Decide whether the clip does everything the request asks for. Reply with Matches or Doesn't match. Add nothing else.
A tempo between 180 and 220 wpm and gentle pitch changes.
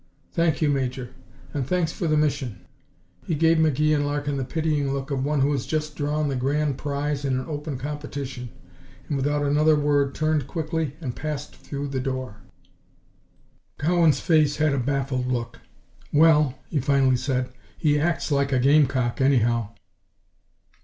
Doesn't match